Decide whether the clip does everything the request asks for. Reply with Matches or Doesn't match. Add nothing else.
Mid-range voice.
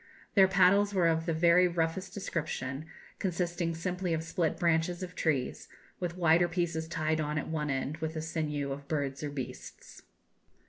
Matches